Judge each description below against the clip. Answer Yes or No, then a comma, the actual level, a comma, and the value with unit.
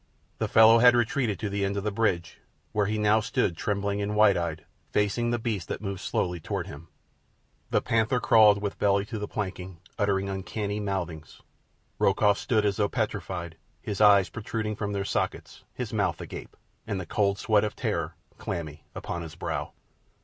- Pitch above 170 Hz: No, low, 100 Hz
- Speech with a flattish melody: Yes, narrow, 2.2 semitones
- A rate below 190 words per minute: Yes, average, 180 wpm